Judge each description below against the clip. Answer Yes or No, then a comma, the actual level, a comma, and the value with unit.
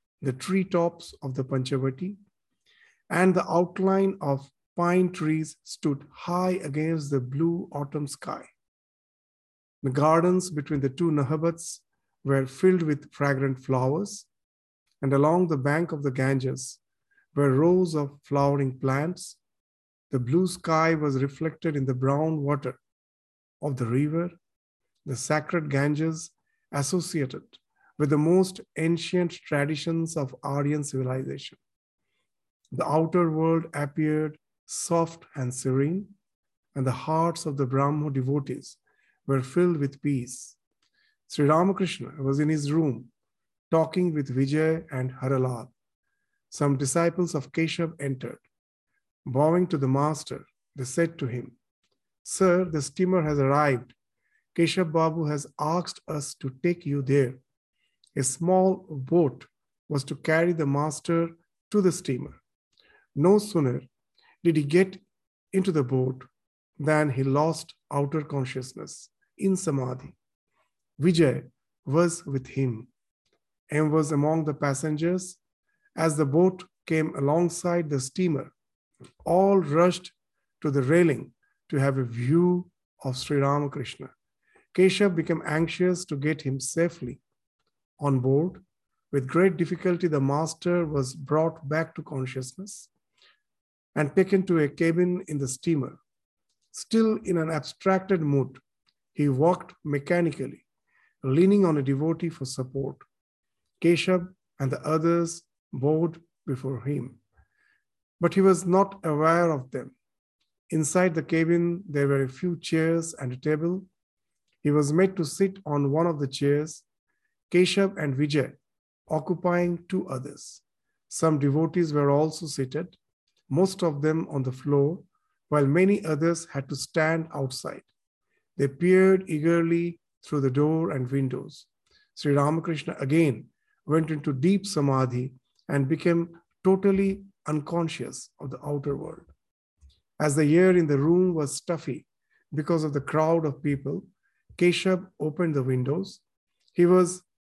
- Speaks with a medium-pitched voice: Yes, medium, 155 Hz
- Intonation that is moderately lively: Yes, average, 3.9 semitones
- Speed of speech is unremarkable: No, slow, 130 wpm